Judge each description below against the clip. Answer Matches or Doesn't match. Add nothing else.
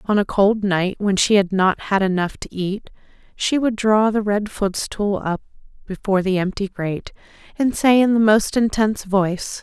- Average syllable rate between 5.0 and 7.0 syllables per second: Doesn't match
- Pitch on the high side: Matches